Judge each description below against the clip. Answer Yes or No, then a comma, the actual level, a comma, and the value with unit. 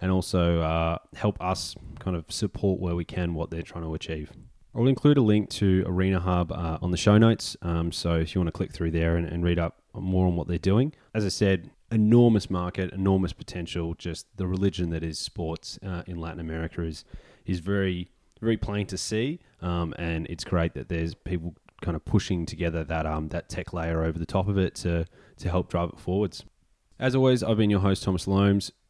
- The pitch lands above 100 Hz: No, very low, 90 Hz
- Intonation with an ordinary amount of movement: Yes, average, 3.0 semitones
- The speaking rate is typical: No, fast, 220 wpm